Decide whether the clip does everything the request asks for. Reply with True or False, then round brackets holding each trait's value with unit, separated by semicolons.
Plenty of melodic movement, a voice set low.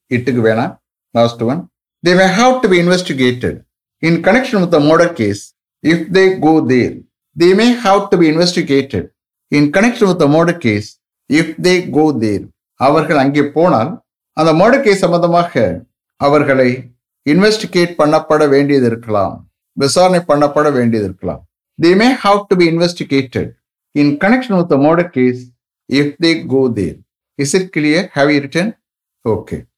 False (5.8 semitones; 155 Hz)